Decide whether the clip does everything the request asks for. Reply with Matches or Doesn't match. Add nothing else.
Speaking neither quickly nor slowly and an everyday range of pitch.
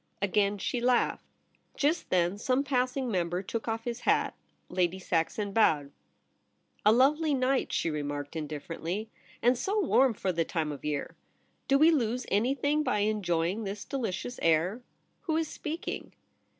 Doesn't match